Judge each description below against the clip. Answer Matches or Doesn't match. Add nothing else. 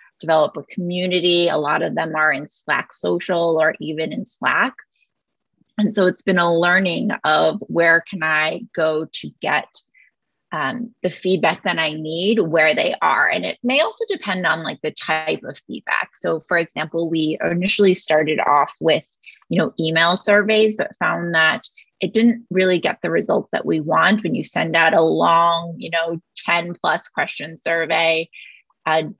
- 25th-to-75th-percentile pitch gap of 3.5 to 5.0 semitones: Doesn't match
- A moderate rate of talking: Matches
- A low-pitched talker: Doesn't match